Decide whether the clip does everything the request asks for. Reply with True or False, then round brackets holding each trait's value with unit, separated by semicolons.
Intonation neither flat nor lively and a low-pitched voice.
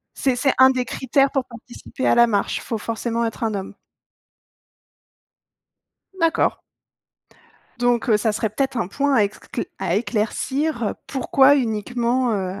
False (3.4 semitones; 240 Hz)